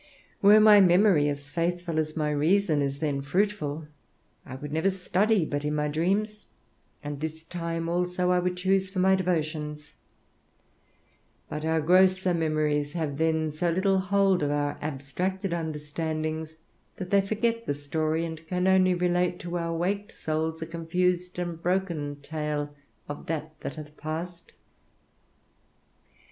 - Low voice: No, medium, 165 Hz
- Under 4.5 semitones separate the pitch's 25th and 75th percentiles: Yes, average, 3.2 semitones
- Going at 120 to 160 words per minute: Yes, average, 150 wpm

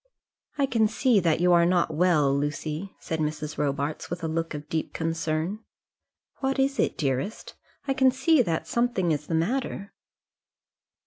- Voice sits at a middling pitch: Yes, medium, 170 Hz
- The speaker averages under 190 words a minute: Yes, average, 165 wpm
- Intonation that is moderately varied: No, wide, 6.3 semitones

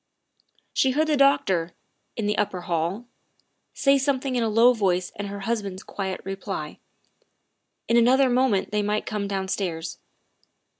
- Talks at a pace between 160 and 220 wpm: No, average, 150 wpm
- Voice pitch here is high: Yes, high, 210 Hz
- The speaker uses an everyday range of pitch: Yes, average, 4.7 semitones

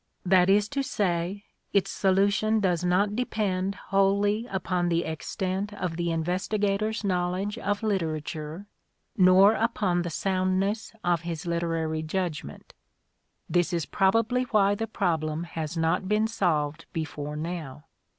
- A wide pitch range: No, average, 3.4 semitones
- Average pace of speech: No, slow, 130 wpm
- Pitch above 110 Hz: Yes, medium, 185 Hz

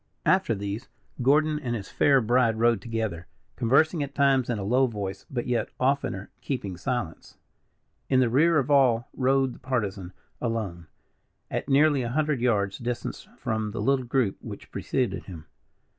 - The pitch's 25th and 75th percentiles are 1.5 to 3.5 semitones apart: No, average, 4.3 semitones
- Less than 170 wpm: Yes, average, 160 wpm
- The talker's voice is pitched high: No, low, 120 Hz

